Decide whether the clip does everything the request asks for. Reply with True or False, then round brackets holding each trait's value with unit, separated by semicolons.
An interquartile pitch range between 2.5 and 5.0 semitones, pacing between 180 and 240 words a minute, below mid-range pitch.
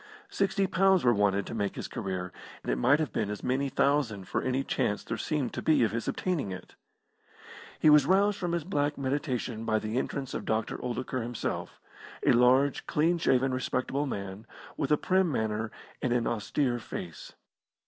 False (5.4 semitones; 185 wpm; 130 Hz)